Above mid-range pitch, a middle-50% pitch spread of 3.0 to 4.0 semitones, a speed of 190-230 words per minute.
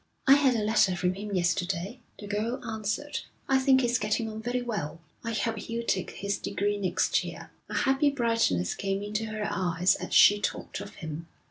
Yes: high, 210 Hz; average, 3.3 semitones; average, 195 wpm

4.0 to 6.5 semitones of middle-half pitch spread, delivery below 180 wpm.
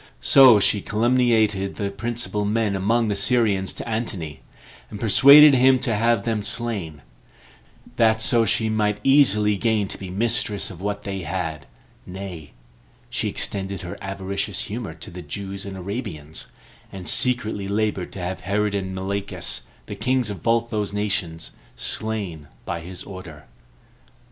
No: average, 3.1 semitones; average, 150 wpm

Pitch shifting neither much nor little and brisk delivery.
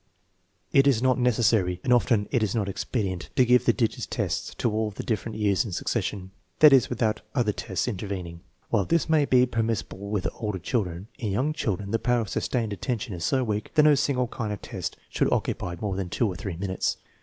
Yes: average, 4.1 semitones; fast, 215 wpm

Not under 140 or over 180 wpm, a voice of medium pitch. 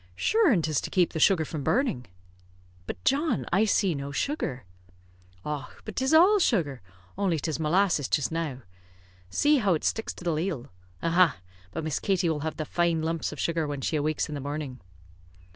No: average, 190 wpm; medium, 165 Hz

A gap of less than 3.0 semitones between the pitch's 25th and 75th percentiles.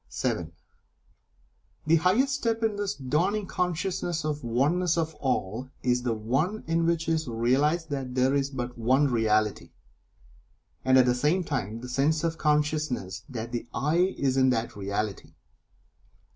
No: average, 5.3 semitones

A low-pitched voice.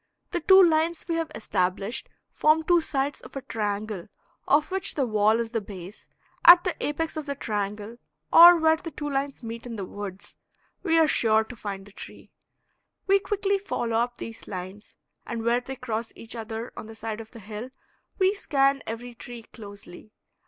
No: high, 235 Hz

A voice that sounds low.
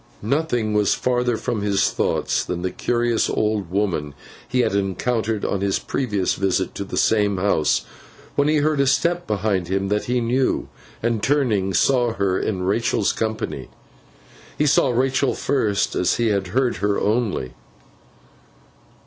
Yes: low, 110 Hz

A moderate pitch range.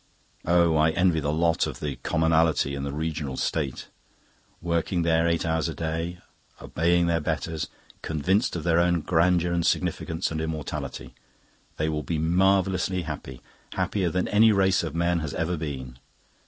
No: narrow, 1.9 semitones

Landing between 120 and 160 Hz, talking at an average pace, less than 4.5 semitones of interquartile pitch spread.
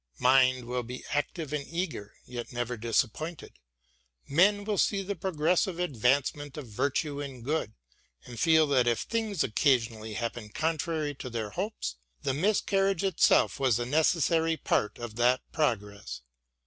No: medium, 140 Hz; average, 150 wpm; wide, 5.5 semitones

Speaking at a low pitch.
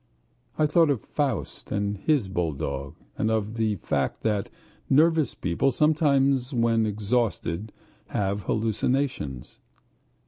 Yes: low, 110 Hz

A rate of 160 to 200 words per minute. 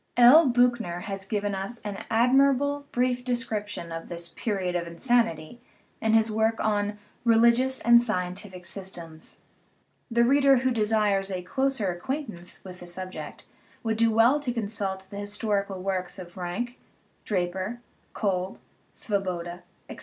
No: average, 140 wpm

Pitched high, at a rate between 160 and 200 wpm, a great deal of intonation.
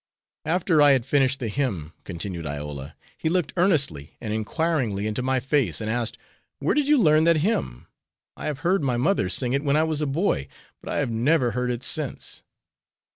No: low, 130 Hz; average, 195 wpm; wide, 6.4 semitones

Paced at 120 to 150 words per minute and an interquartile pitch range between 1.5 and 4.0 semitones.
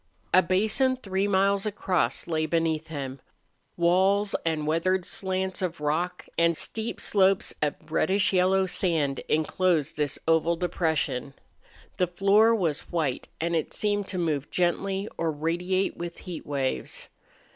Yes: slow, 135 wpm; average, 3.3 semitones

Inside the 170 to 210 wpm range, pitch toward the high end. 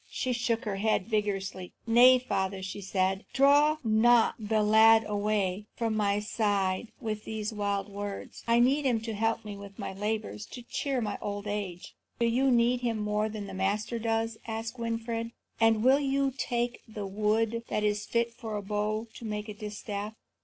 Yes: average, 180 wpm; high, 215 Hz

